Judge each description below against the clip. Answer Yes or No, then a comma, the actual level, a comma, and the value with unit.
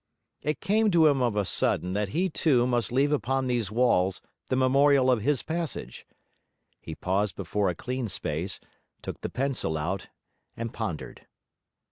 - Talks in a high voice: No, low, 125 Hz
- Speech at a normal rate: Yes, average, 160 wpm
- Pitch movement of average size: No, wide, 5.9 semitones